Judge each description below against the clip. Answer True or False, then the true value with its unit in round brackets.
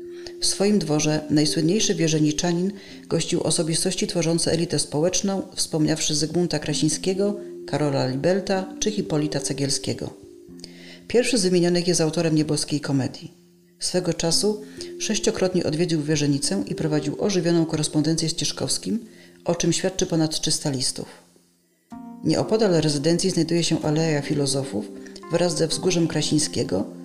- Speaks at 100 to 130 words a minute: True (115 wpm)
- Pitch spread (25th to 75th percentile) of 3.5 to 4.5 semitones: False (3.1 semitones)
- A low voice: False (160 Hz)